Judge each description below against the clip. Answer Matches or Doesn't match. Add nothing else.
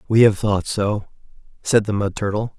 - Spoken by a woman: Doesn't match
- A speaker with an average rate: Matches